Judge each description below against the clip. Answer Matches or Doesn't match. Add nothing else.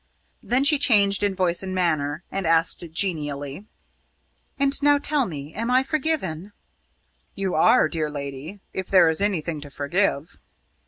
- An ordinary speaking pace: Matches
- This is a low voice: Doesn't match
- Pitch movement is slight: Doesn't match